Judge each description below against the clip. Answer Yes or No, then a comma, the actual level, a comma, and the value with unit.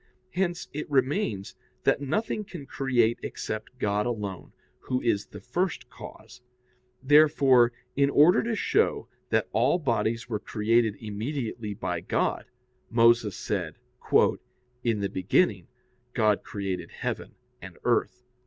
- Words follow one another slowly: Yes, slow, 125 wpm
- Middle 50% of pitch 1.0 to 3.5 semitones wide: No, wide, 5.4 semitones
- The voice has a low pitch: Yes, low, 120 Hz